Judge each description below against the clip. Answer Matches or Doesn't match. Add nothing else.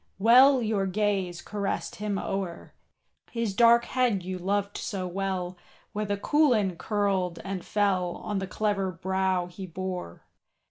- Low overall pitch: Doesn't match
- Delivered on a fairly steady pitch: Matches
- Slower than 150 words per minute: Matches